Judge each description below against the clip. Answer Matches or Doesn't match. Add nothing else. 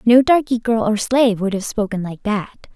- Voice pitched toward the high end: Matches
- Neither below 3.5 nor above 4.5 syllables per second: Doesn't match